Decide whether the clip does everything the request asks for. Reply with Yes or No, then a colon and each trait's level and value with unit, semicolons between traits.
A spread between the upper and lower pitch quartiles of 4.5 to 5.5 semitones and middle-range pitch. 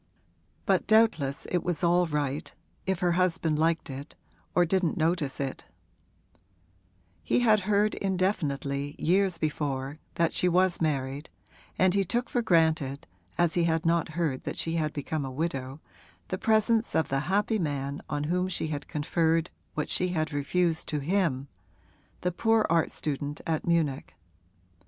No: average, 3.8 semitones; medium, 165 Hz